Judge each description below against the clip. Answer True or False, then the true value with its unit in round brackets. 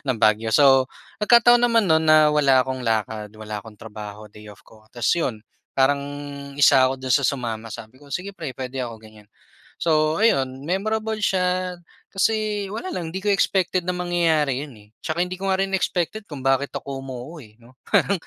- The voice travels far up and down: True (7.2 semitones)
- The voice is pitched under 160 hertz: True (140 Hz)